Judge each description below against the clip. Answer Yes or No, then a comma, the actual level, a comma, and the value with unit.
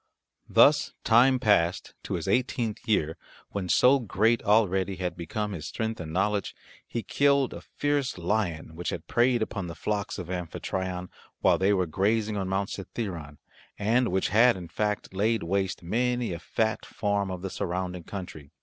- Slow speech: No, average, 170 wpm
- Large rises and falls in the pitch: No, average, 3.9 semitones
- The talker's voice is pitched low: Yes, low, 100 Hz